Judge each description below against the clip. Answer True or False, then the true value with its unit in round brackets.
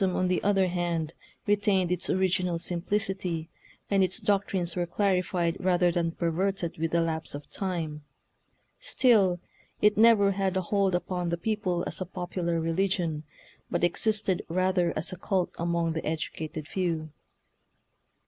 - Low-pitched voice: False (180 Hz)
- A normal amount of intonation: False (2.3 semitones)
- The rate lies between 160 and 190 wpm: False (150 wpm)